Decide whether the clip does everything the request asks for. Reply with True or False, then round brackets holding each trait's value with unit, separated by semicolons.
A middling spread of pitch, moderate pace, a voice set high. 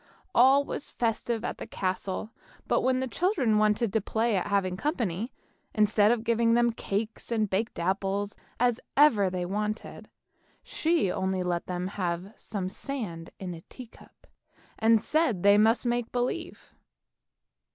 True (3.9 semitones; 160 wpm; 215 Hz)